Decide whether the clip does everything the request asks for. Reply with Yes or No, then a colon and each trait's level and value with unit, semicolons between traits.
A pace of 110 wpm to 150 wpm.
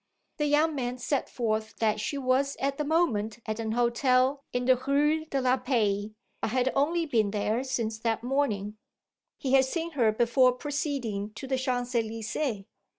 No: average, 175 wpm